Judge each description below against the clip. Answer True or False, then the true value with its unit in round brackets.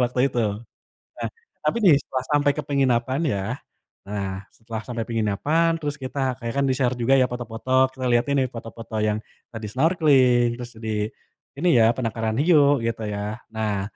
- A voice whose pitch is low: True (120 Hz)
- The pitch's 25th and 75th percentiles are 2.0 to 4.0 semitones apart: True (3.6 semitones)